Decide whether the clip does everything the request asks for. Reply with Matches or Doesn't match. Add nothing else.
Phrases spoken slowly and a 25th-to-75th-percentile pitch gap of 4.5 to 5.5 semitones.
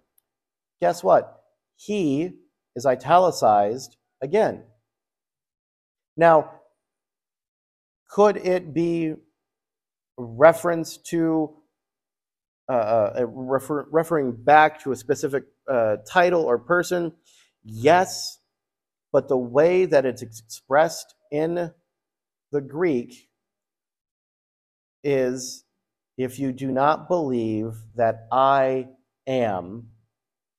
Matches